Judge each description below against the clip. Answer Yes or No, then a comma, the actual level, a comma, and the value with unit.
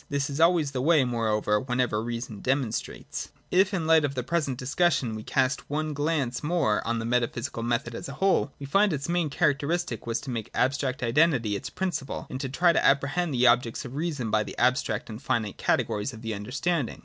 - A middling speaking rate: No, fast, 210 wpm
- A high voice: No, low, 135 Hz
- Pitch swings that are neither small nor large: Yes, average, 4.6 semitones